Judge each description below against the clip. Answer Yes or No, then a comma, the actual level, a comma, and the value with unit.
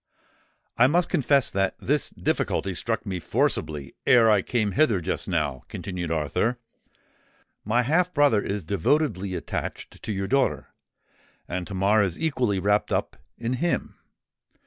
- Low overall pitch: Yes, low, 105 Hz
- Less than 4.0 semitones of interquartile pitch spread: No, wide, 5.4 semitones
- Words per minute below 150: Yes, average, 140 wpm